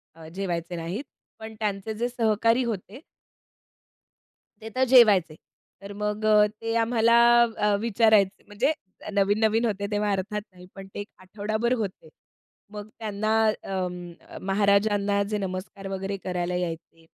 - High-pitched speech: Yes, high, 205 Hz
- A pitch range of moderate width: No, narrow, 2.3 semitones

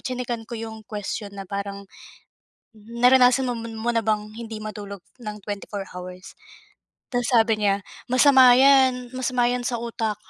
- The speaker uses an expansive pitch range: No, average, 2.9 semitones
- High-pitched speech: Yes, high, 225 Hz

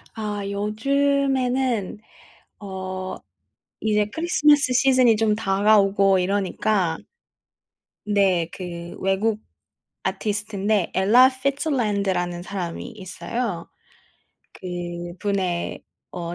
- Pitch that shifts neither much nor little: Yes, average, 3.6 semitones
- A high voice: Yes, high, 205 Hz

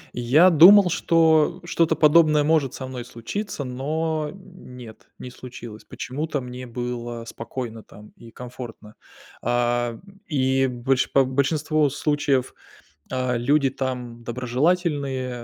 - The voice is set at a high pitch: No, low, 130 Hz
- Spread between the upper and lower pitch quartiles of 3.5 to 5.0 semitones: Yes, average, 4.1 semitones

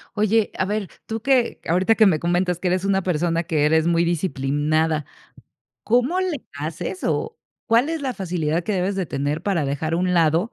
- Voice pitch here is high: No, medium, 180 Hz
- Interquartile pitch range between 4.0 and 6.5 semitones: Yes, average, 5.1 semitones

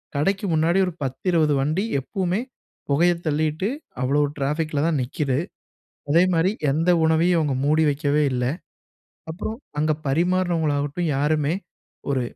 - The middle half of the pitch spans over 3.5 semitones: No, average, 3.2 semitones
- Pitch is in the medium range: Yes, medium, 155 Hz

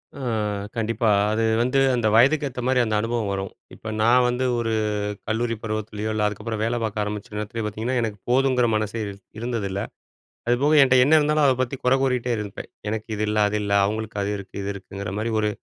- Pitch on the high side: No, low, 115 Hz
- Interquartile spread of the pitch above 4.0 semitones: No, average, 2.8 semitones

